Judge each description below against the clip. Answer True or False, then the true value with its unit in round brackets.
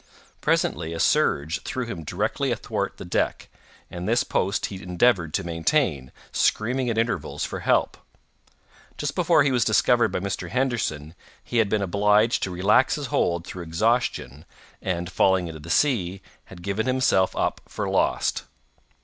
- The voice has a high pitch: False (100 Hz)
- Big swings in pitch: True (5.7 semitones)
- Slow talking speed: False (160 wpm)